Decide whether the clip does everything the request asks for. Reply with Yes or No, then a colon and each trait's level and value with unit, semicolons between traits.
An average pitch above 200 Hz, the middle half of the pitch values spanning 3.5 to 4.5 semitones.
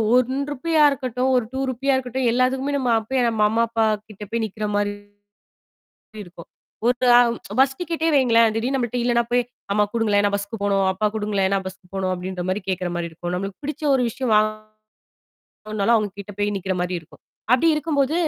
Yes: high, 225 Hz; average, 4.2 semitones